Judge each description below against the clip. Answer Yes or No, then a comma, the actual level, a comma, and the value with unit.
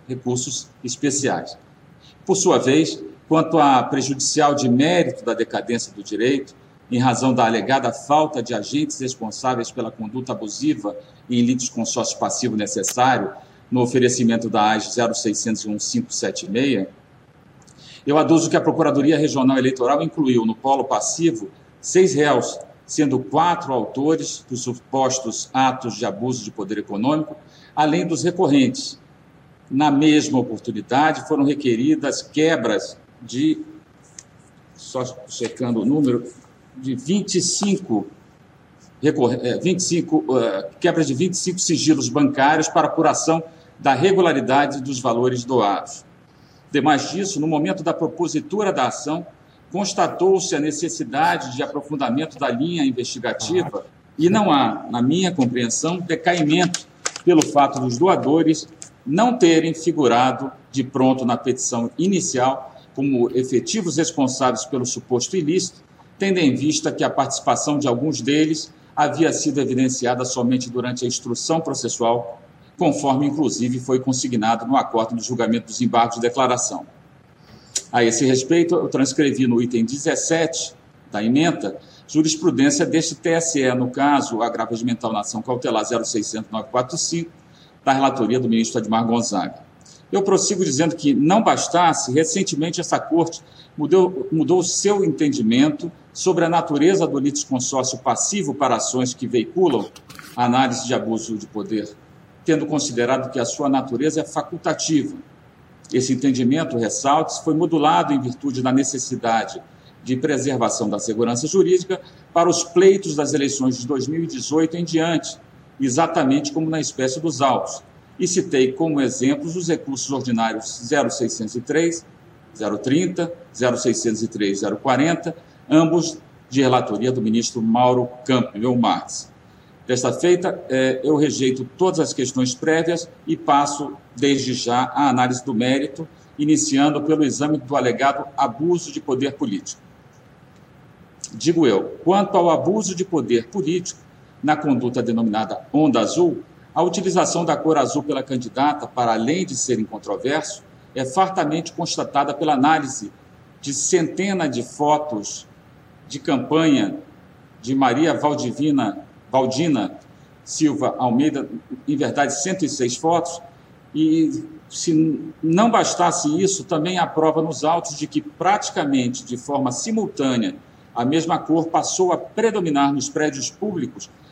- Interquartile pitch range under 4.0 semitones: No, average, 4.6 semitones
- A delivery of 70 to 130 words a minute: Yes, average, 125 wpm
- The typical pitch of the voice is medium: Yes, medium, 145 Hz